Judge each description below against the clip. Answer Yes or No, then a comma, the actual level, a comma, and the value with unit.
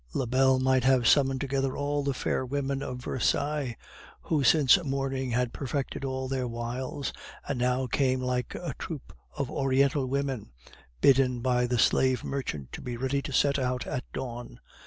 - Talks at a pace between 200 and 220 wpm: No, average, 165 wpm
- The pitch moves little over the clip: Yes, narrow, 1.6 semitones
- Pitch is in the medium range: No, low, 130 Hz